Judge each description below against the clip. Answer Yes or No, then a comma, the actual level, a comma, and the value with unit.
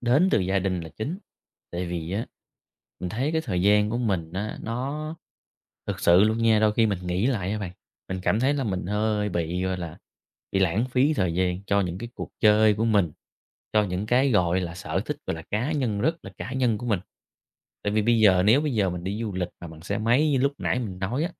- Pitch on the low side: Yes, low, 105 Hz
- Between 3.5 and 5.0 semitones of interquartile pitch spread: Yes, average, 4.6 semitones